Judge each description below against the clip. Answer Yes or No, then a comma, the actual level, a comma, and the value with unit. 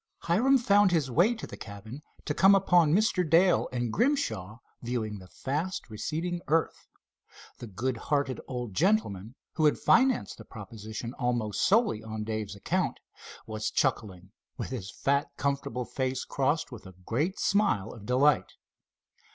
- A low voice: Yes, low, 130 Hz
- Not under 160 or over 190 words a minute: No, average, 150 wpm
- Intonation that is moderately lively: No, wide, 8.0 semitones